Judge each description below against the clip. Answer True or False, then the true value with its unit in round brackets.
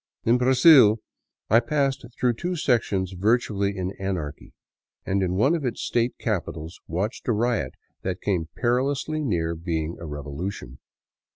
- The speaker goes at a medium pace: True (150 wpm)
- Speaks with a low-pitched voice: True (105 Hz)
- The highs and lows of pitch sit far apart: True (6.0 semitones)